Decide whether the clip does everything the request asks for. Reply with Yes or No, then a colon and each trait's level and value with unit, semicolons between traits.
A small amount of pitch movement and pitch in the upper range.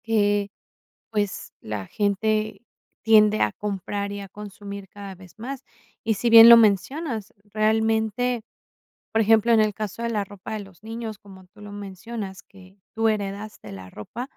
Yes: narrow, 2.0 semitones; high, 210 Hz